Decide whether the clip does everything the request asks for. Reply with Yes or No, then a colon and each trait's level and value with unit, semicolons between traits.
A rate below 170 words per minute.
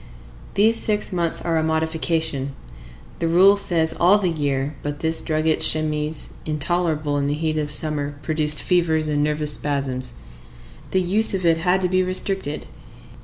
Yes: average, 160 wpm